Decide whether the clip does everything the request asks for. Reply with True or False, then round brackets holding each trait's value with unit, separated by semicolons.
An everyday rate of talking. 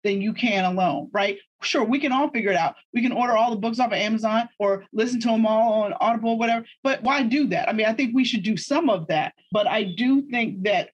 False (270 wpm)